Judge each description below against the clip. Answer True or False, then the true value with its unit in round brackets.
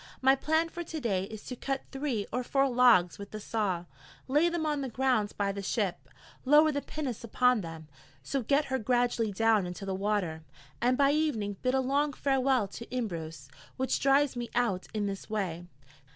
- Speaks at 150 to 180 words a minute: False (195 wpm)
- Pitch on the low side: False (245 Hz)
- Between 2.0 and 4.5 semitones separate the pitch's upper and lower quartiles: False (5.2 semitones)